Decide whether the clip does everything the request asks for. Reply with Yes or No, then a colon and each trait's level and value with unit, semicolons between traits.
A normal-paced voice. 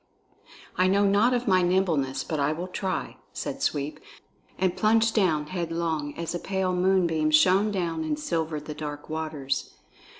Yes: average, 160 wpm